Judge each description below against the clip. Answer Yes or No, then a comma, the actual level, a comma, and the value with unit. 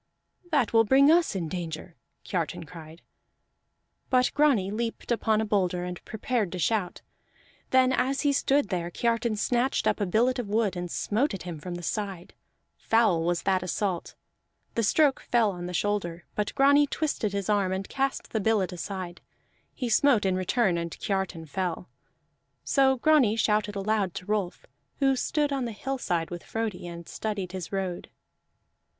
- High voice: Yes, high, 205 Hz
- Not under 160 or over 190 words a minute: Yes, average, 170 wpm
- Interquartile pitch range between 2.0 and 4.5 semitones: No, wide, 5.4 semitones